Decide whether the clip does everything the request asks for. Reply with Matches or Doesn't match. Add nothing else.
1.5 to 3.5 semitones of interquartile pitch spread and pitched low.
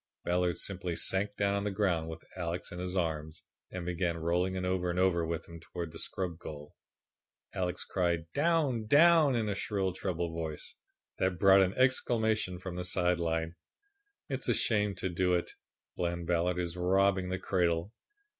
Matches